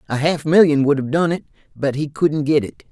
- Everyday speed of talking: No, fast, 245 wpm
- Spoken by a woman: No, male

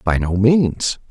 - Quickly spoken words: No, average, 160 wpm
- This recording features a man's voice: Yes, male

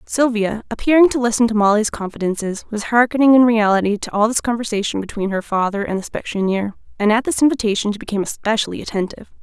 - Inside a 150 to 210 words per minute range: Yes, average, 185 wpm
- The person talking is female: Yes, female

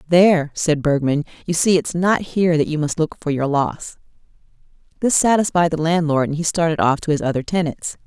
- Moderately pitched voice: Yes, medium, 160 Hz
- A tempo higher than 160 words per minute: Yes, average, 200 wpm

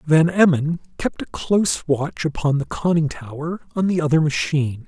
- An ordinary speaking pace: Yes, average, 170 wpm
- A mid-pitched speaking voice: Yes, medium, 150 Hz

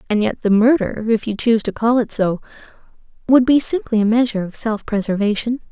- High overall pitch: Yes, high, 225 Hz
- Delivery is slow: No, average, 200 wpm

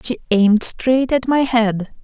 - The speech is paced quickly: No, average, 175 wpm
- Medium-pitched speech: No, high, 240 Hz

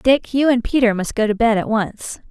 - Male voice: No, female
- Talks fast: Yes, fast, 260 wpm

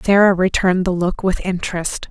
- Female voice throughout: Yes, female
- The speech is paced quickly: No, average, 170 wpm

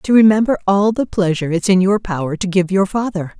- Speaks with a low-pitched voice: No, high, 190 Hz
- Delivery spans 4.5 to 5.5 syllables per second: No, 5.9 syllables/s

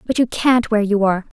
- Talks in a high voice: Yes, high, 220 Hz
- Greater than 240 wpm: Yes, fast, 260 wpm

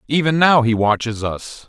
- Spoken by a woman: No, male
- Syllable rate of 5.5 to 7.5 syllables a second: No, 4.6 syllables/s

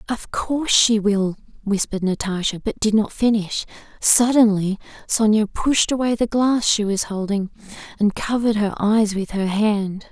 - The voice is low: No, high, 210 Hz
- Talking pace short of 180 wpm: Yes, average, 155 wpm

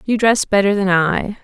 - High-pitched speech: Yes, high, 200 Hz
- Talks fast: Yes, fast, 210 wpm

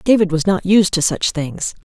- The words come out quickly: Yes, fast, 225 wpm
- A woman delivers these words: Yes, female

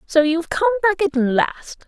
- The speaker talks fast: Yes, fast, 225 wpm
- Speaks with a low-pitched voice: No, very high, 300 Hz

